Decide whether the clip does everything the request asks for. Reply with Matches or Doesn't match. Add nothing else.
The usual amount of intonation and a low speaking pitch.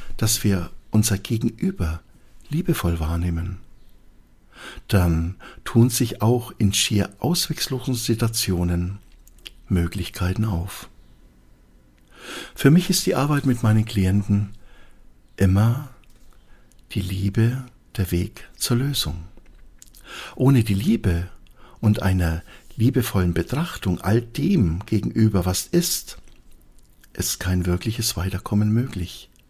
Doesn't match